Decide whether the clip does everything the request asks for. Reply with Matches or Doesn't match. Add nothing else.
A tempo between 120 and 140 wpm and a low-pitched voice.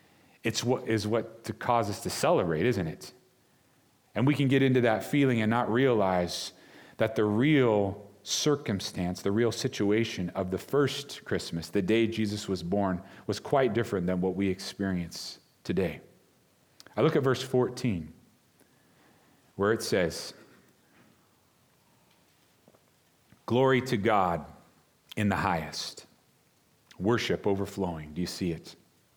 Matches